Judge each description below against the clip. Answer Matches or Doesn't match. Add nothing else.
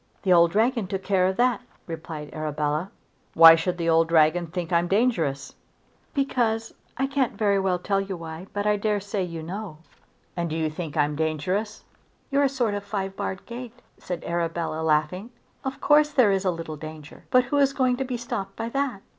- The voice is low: Doesn't match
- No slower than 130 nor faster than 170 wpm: Doesn't match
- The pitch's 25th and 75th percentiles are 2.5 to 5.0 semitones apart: Doesn't match